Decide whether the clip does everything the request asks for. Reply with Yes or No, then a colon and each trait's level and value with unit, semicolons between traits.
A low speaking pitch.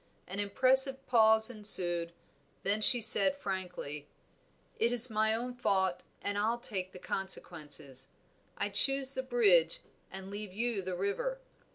No: high, 205 Hz